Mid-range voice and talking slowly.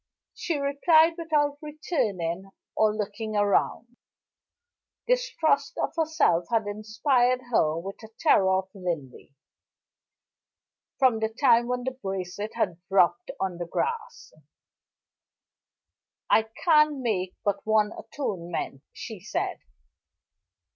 No: high, 220 Hz; slow, 105 wpm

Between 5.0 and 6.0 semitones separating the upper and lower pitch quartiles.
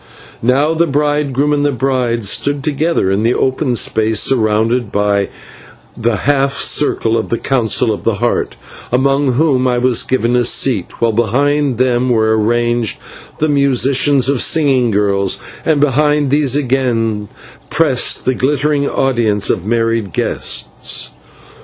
No: average, 3.8 semitones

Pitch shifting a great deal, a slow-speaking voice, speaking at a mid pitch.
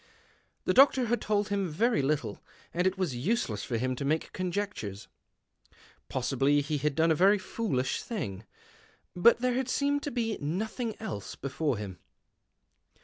No: wide, 8.6 semitones; average, 155 wpm; medium, 175 Hz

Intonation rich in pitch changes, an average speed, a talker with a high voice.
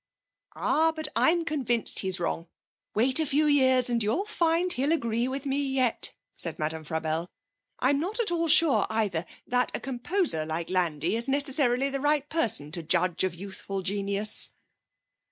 Yes: wide, 7.9 semitones; average, 170 wpm; high, 245 Hz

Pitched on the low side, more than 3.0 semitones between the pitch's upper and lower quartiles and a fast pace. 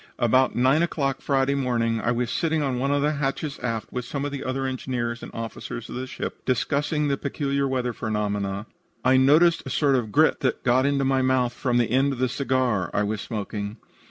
No: low, 130 Hz; average, 2.7 semitones; fast, 215 wpm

